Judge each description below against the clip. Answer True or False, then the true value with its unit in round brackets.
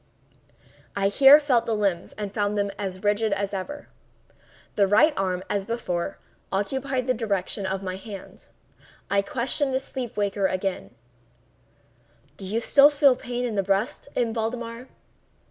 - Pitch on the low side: False (210 Hz)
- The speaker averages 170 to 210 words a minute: False (150 wpm)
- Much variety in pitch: False (4.1 semitones)